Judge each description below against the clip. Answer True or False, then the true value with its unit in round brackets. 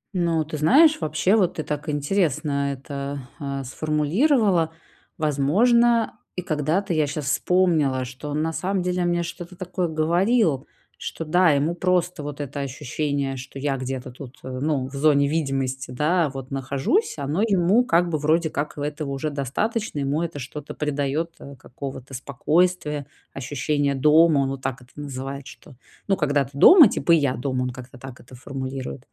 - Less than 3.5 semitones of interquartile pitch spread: False (3.8 semitones)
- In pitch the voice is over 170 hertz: False (150 Hz)